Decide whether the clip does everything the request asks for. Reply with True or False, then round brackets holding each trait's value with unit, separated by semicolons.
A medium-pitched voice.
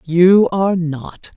True (175 Hz)